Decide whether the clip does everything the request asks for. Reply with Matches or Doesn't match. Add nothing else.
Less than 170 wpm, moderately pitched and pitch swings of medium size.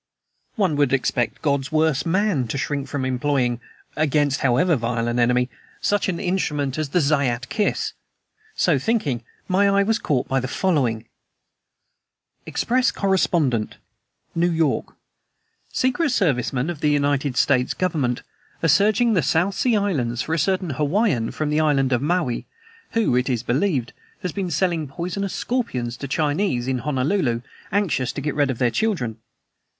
Doesn't match